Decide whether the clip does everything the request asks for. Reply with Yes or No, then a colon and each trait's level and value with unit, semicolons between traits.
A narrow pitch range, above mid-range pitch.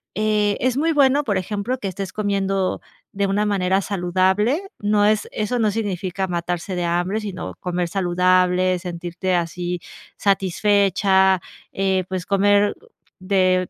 Yes: narrow, 2.2 semitones; high, 195 Hz